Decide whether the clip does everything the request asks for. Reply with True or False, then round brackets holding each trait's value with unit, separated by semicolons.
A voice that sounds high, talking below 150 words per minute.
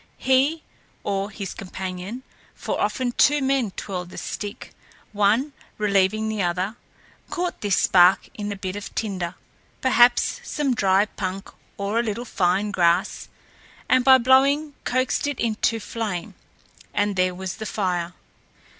True (205 Hz; 140 wpm)